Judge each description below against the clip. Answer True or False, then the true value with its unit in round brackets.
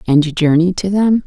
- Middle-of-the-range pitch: True (175 Hz)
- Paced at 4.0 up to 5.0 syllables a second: False (5.3 syllables/s)